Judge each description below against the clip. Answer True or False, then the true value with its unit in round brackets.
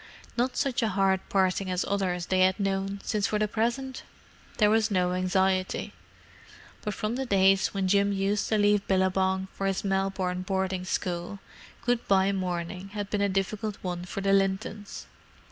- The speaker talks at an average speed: True (170 wpm)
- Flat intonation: True (1.7 semitones)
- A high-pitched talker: True (195 Hz)